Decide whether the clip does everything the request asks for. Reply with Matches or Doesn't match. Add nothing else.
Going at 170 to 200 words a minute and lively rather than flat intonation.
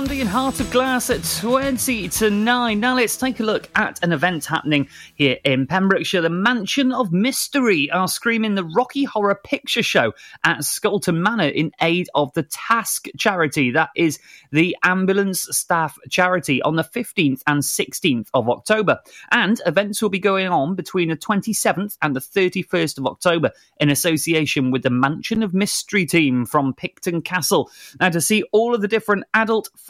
Matches